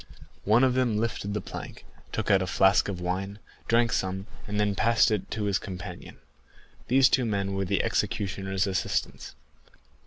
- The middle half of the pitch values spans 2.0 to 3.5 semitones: Yes, narrow, 2.4 semitones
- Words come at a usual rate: Yes, average, 165 wpm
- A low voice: Yes, low, 100 Hz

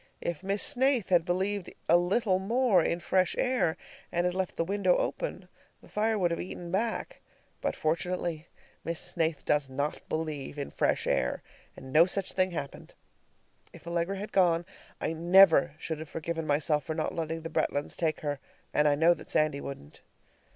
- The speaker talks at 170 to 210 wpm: Yes, average, 180 wpm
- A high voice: No, medium, 170 Hz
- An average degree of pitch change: Yes, average, 3.3 semitones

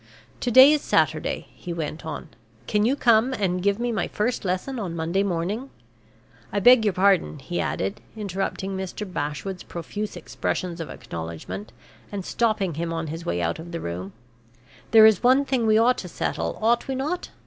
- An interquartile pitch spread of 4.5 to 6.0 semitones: Yes, average, 5.3 semitones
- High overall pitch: Yes, high, 195 Hz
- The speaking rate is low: No, average, 180 wpm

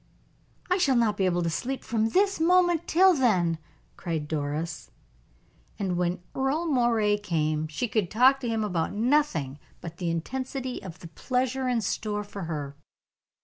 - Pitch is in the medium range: No, high, 210 Hz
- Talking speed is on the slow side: No, average, 160 wpm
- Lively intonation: Yes, wide, 7.8 semitones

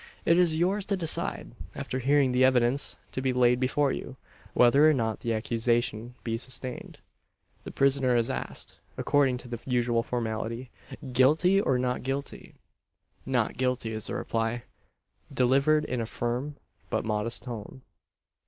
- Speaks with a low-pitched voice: Yes, low, 125 Hz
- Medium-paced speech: Yes, average, 150 wpm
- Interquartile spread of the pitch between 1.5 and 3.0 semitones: Yes, average, 2.7 semitones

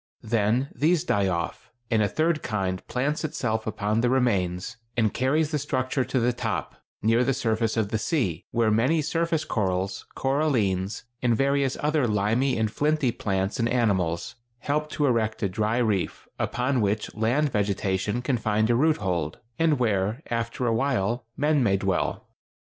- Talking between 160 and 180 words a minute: Yes, average, 165 wpm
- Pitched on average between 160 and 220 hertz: No, low, 115 Hz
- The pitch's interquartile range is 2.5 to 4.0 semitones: No, average, 4.8 semitones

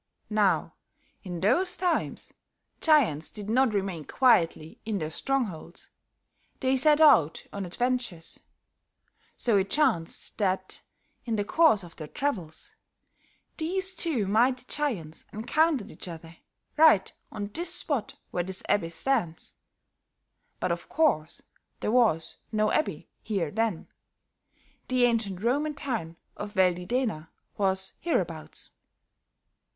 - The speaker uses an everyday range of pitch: No, wide, 7.1 semitones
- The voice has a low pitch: No, high, 210 Hz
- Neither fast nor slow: No, slow, 120 wpm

